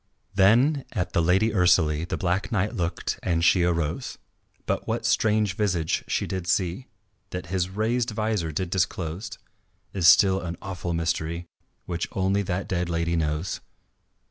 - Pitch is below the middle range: Yes, very low, 90 Hz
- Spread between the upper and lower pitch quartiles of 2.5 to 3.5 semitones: Yes, average, 2.9 semitones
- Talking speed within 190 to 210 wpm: No, average, 150 wpm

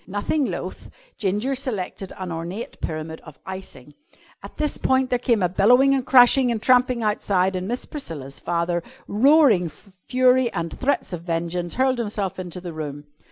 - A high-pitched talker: Yes, high, 200 Hz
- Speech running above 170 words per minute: No, average, 160 wpm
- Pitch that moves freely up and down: Yes, wide, 6.6 semitones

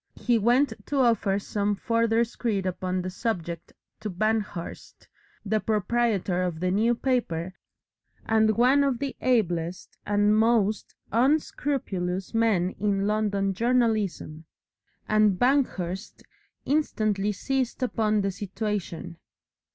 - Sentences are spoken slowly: Yes, slow, 110 wpm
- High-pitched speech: Yes, high, 215 Hz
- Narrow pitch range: No, average, 3.8 semitones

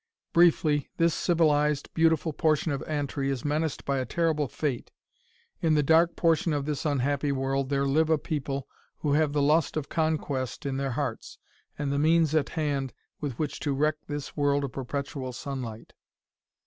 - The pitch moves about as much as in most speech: No, narrow, 2.3 semitones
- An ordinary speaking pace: Yes, average, 175 wpm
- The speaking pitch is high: No, medium, 145 Hz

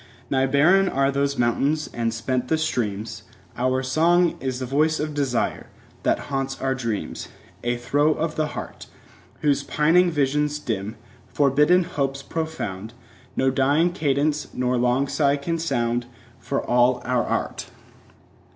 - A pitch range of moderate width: Yes, average, 3.4 semitones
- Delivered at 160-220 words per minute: No, average, 145 wpm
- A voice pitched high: No, low, 135 Hz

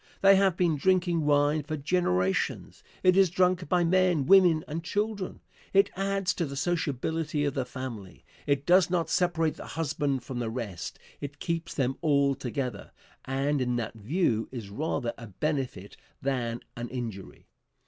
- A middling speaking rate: Yes, average, 160 wpm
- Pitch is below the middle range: No, medium, 145 Hz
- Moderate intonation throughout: No, wide, 5.8 semitones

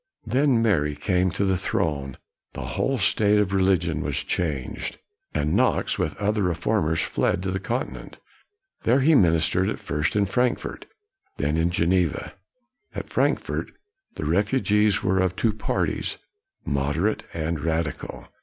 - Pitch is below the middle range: Yes, very low, 95 Hz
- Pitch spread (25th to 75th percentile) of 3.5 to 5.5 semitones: Yes, average, 4.6 semitones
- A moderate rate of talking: Yes, average, 145 wpm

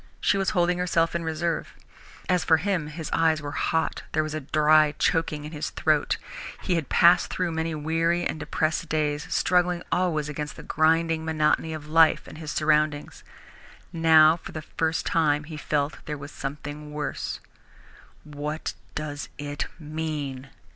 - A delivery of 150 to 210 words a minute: Yes, average, 165 wpm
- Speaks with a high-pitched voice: No, medium, 155 Hz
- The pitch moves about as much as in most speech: No, narrow, 1.7 semitones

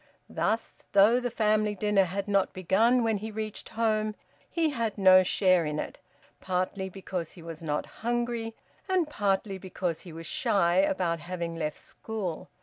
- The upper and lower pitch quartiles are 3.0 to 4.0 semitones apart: Yes, average, 3.5 semitones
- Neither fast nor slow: Yes, average, 160 wpm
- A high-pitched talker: Yes, high, 195 Hz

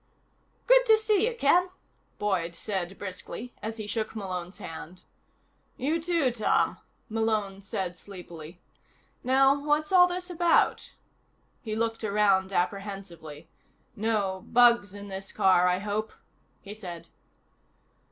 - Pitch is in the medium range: No, high, 210 Hz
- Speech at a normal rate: No, slow, 125 wpm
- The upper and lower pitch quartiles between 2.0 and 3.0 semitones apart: No, wide, 5.5 semitones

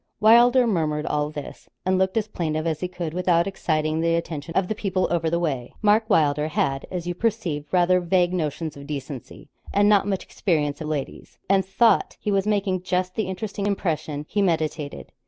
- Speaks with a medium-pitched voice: Yes, medium, 175 Hz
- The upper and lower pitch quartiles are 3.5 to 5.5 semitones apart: Yes, average, 4.1 semitones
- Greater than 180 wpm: Yes, average, 190 wpm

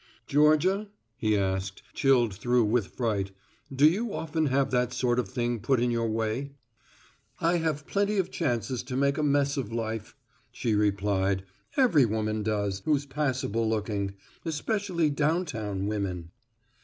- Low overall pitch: Yes, low, 125 Hz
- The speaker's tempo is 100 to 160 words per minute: Yes, average, 145 wpm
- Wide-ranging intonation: Yes, wide, 5.7 semitones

